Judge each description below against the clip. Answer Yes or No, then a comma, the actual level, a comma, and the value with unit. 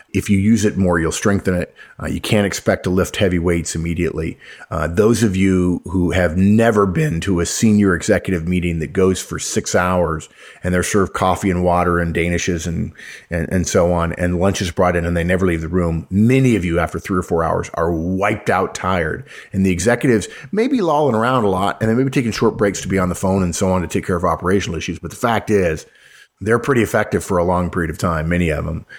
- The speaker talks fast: Yes, fast, 240 wpm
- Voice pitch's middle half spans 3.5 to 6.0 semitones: No, average, 2.7 semitones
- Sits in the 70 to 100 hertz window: Yes, very low, 90 Hz